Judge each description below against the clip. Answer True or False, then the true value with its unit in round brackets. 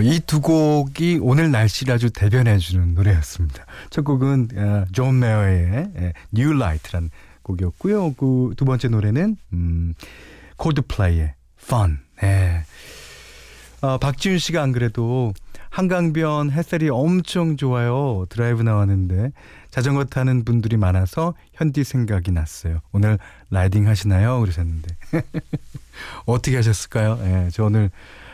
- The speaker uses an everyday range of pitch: False (7.0 semitones)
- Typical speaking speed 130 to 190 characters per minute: False (285 characters per minute)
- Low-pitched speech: True (115 Hz)